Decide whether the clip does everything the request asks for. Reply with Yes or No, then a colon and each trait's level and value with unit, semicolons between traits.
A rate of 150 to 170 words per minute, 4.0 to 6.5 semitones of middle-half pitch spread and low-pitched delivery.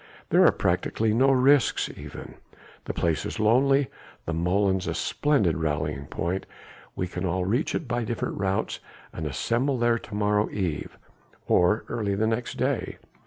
Yes: average, 160 wpm; average, 5.3 semitones; low, 105 Hz